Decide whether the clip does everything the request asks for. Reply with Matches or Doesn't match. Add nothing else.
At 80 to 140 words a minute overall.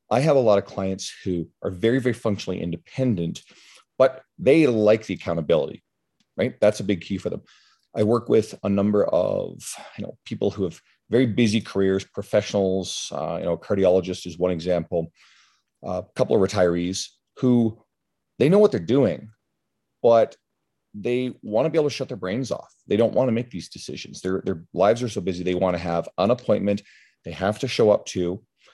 Doesn't match